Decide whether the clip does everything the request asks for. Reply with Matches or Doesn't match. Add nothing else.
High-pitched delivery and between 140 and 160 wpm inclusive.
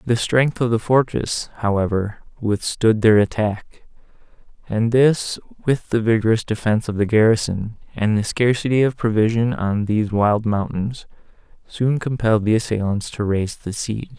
Doesn't match